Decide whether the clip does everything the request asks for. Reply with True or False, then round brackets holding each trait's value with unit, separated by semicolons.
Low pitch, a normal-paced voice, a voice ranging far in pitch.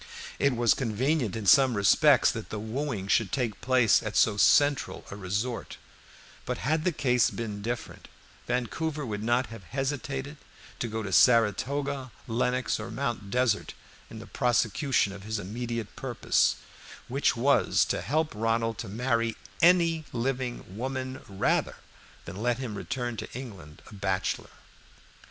False (120 Hz; 145 wpm; 3.7 semitones)